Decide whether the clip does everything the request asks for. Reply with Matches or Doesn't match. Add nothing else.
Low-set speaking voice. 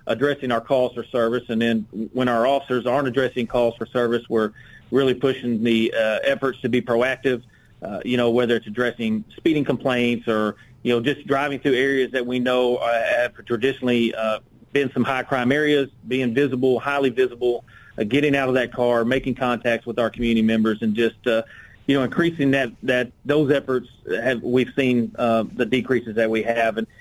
Matches